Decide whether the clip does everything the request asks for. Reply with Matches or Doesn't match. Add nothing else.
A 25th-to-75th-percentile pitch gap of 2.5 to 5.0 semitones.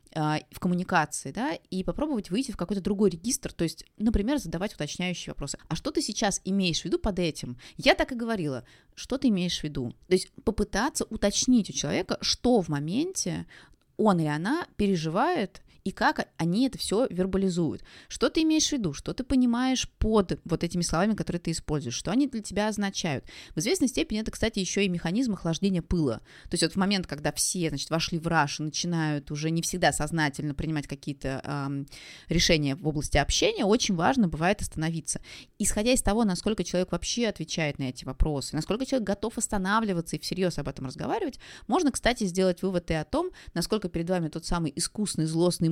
Doesn't match